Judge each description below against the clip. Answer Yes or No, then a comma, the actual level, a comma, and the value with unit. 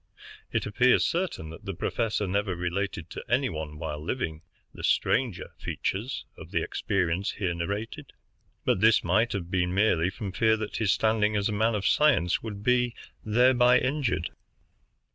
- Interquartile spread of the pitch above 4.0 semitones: Yes, average, 4.6 semitones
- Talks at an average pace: Yes, average, 160 wpm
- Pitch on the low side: Yes, low, 105 Hz